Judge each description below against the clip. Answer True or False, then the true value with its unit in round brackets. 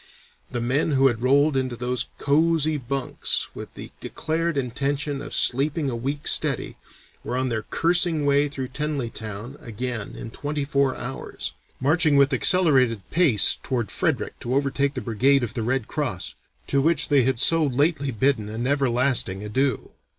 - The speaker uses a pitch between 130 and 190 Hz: True (135 Hz)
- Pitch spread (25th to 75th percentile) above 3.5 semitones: False (3.1 semitones)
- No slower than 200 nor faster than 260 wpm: False (160 wpm)